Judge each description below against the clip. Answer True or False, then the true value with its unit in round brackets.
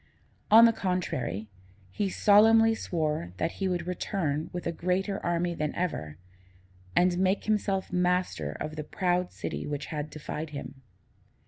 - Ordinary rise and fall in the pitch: True (3.9 semitones)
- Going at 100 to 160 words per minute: True (145 wpm)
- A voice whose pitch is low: False (175 Hz)